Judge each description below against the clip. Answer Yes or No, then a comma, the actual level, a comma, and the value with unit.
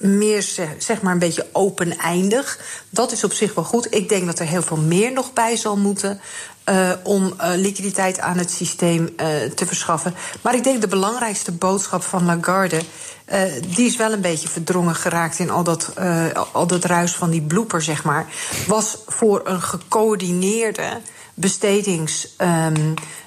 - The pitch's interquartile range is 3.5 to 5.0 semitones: No, average, 3.1 semitones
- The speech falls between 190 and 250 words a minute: No, average, 170 wpm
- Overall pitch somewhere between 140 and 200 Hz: Yes, medium, 185 Hz